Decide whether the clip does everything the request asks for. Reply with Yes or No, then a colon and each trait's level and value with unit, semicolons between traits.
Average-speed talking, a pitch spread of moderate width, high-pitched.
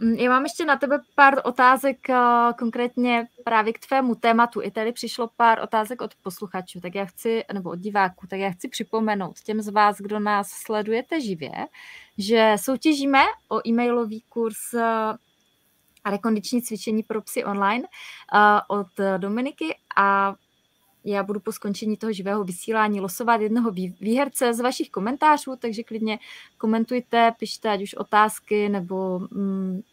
Yes: average, 140 wpm; average, 3.0 semitones; high, 225 Hz